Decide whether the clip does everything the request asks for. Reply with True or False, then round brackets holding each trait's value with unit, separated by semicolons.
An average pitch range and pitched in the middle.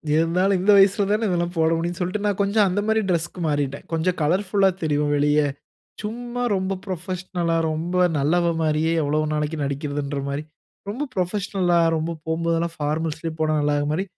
True (3.6 semitones; 170 Hz)